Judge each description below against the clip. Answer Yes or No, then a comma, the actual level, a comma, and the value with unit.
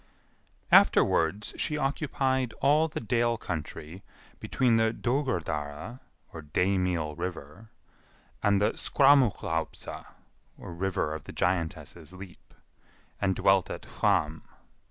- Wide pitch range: Yes, wide, 6.9 semitones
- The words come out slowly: Yes, slow, 100 wpm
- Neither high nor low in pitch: No, very low, 95 Hz